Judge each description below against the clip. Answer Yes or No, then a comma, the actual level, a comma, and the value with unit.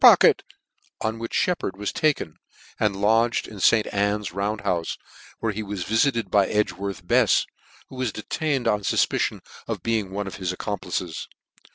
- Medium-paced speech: Yes, average, 160 wpm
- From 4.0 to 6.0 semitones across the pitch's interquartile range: No, narrow, 2.6 semitones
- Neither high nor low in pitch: No, low, 105 Hz